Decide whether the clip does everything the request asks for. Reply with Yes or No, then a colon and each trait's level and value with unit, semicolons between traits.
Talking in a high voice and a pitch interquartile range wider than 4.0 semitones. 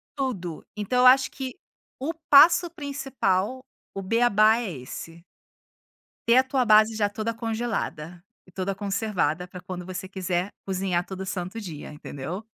Yes: high, 205 Hz; average, 5.0 semitones